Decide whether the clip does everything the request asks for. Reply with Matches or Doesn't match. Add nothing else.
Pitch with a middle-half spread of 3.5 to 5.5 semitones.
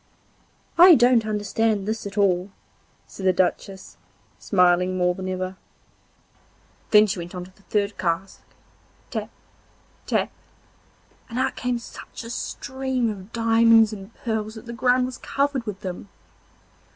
Matches